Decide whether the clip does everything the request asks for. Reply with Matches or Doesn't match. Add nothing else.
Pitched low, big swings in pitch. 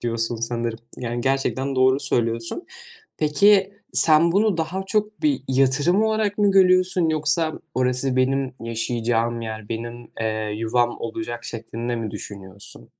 Matches